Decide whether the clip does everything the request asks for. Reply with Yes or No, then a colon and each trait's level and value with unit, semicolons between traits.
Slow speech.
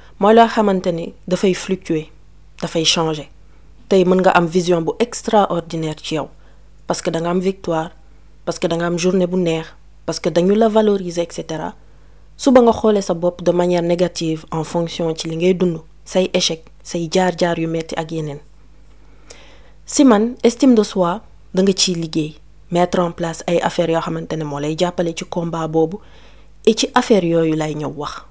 Yes: slow, 140 wpm